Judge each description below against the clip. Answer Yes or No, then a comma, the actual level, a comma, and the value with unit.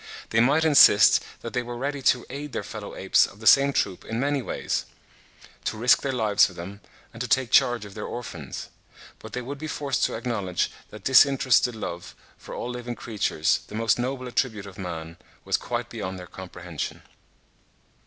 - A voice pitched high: No, low, 120 Hz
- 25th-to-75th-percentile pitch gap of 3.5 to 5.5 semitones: Yes, average, 4.7 semitones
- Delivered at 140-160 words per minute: No, average, 190 wpm